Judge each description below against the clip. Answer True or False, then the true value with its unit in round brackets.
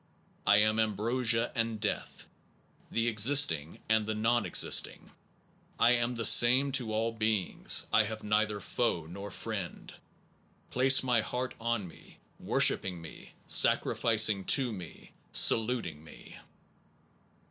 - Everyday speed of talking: False (125 wpm)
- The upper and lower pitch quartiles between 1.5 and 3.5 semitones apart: True (2.4 semitones)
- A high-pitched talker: False (110 Hz)